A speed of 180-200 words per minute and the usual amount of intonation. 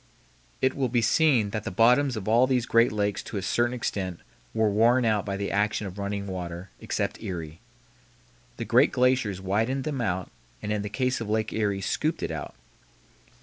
Yes: average, 195 wpm; average, 3.7 semitones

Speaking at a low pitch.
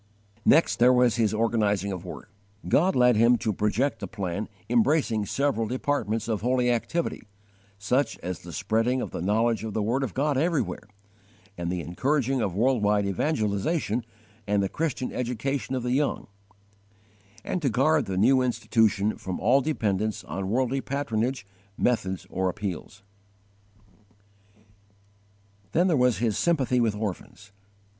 Yes: low, 115 Hz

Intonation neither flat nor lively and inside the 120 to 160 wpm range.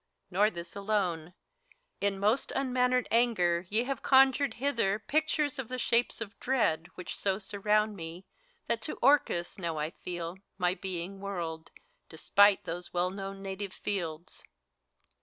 Yes: average, 5.0 semitones; average, 140 wpm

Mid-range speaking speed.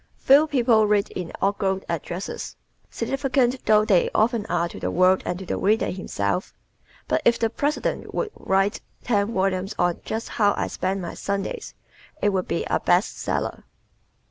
Yes: average, 165 wpm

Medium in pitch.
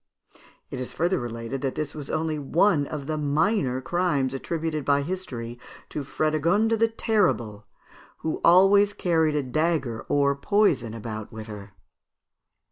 Yes: medium, 150 Hz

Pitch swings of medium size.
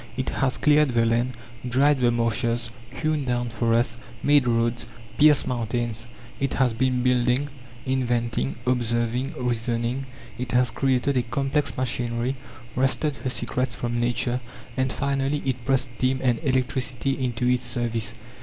No: narrow, 2.1 semitones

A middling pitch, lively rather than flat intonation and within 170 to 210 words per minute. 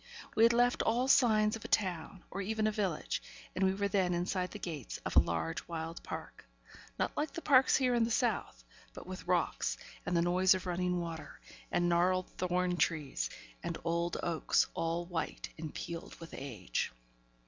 No: medium, 180 Hz; average, 4.1 semitones; average, 180 wpm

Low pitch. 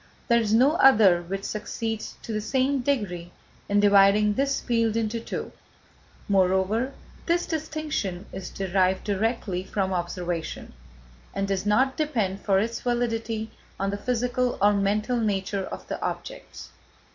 No: high, 210 Hz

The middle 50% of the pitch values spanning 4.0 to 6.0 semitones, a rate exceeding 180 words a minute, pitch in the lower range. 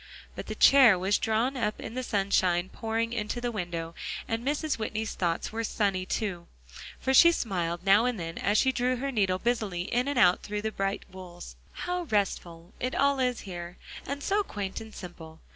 No: average, 5.1 semitones; average, 195 wpm; high, 215 Hz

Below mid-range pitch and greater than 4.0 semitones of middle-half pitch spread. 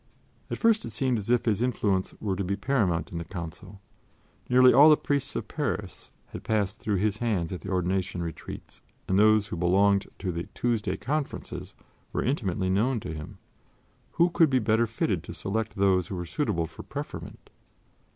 Yes: low, 100 Hz; average, 4.4 semitones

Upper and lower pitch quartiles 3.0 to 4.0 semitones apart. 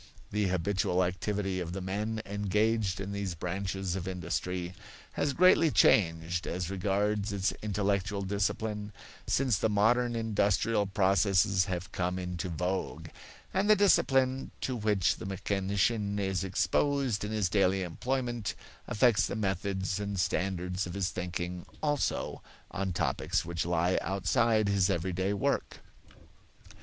No: narrow, 2.6 semitones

